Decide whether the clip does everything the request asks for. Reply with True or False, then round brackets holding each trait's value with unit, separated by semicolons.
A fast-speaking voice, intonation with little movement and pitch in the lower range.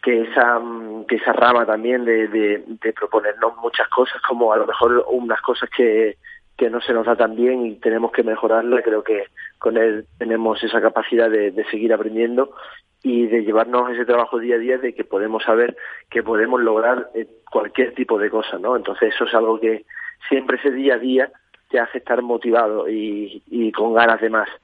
True (195 wpm; 1.6 semitones; 115 Hz)